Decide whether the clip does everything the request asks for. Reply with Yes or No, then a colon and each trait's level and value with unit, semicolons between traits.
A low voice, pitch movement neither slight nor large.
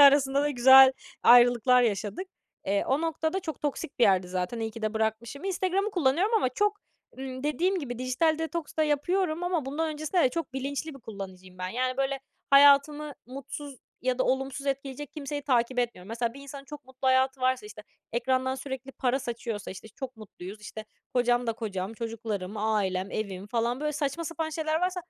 No: very high, 260 Hz; average, 4.5 semitones